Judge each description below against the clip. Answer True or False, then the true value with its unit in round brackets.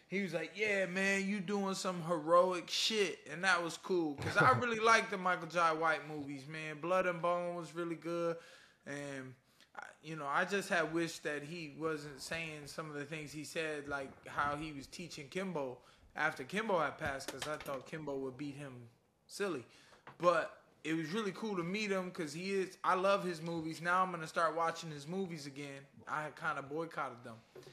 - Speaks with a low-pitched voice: False (165 Hz)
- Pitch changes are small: False (3.6 semitones)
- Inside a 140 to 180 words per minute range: False (205 wpm)